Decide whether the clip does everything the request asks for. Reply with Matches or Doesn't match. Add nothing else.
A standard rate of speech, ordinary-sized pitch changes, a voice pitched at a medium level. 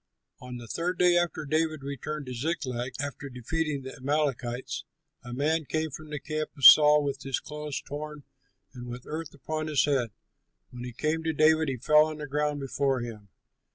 Matches